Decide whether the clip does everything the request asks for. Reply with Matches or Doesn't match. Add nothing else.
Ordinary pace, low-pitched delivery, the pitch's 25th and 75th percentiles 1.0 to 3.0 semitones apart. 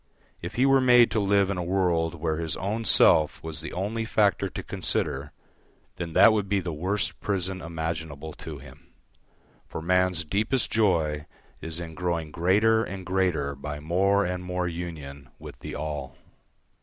Doesn't match